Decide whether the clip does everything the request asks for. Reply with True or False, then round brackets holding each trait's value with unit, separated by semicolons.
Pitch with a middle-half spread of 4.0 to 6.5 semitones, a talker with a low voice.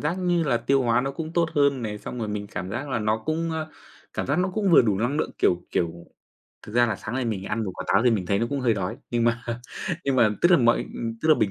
True (5.4 semitones; 120 Hz)